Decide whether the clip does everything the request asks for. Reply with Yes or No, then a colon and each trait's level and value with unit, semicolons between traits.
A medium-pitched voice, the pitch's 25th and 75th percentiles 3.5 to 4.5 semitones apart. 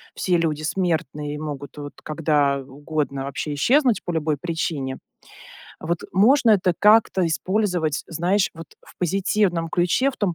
Yes: medium, 165 Hz; average, 4.2 semitones